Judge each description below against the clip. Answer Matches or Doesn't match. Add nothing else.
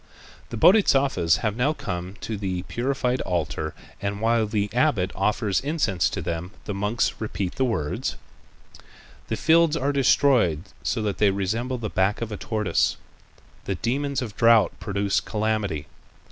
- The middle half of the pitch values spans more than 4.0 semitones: Matches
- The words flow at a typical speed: Matches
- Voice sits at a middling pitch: Doesn't match